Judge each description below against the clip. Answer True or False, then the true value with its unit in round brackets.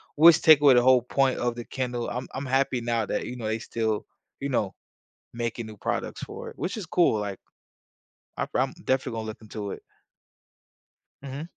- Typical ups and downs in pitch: True (3.5 semitones)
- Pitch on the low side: True (125 Hz)